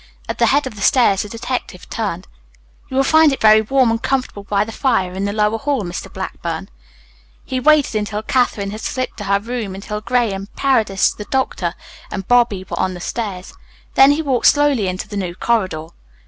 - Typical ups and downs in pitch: Yes, average, 4.6 semitones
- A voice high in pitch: Yes, high, 220 Hz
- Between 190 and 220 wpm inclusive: Yes, average, 200 wpm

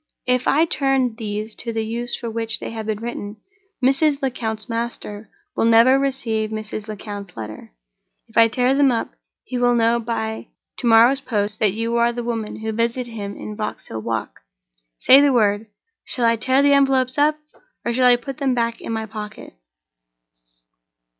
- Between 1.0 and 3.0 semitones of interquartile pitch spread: Yes, average, 2.7 semitones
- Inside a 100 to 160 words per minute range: No, average, 180 wpm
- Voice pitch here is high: Yes, high, 230 Hz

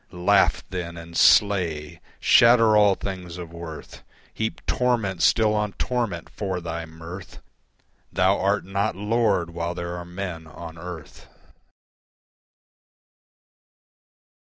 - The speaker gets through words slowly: Yes, slow, 110 wpm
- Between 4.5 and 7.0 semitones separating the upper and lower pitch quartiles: No, average, 3.4 semitones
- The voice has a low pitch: Yes, very low, 90 Hz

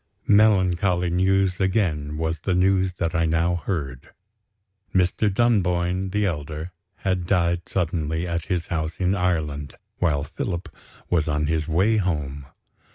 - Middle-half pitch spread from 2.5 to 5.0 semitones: Yes, average, 2.9 semitones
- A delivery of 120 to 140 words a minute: Yes, slow, 135 wpm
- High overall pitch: No, very low, 85 Hz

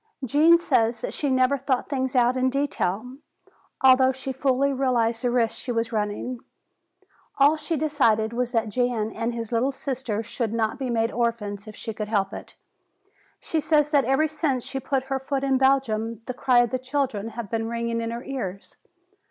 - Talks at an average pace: Yes, average, 185 wpm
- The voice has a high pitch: Yes, very high, 250 Hz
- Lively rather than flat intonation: No, average, 2.9 semitones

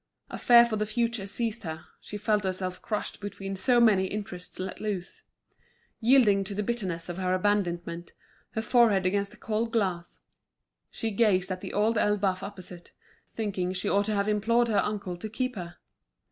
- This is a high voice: Yes, high, 205 Hz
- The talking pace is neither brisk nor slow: Yes, average, 175 wpm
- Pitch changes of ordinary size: Yes, average, 3.0 semitones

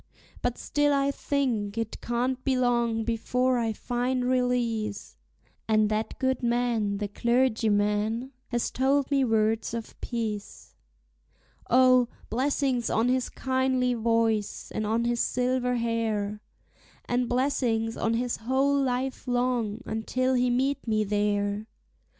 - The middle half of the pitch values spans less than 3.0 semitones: Yes, narrow, 2.5 semitones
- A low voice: No, high, 240 Hz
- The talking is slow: Yes, slow, 125 wpm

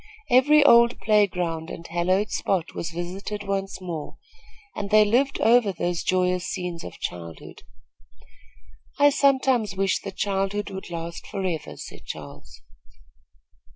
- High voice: Yes, high, 195 Hz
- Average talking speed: No, slow, 125 wpm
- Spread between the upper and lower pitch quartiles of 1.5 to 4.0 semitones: Yes, average, 3.5 semitones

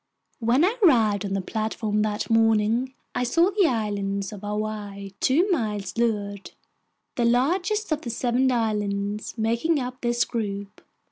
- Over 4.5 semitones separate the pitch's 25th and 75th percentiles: No, average, 3.6 semitones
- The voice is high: Yes, high, 225 Hz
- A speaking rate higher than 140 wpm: Yes, average, 150 wpm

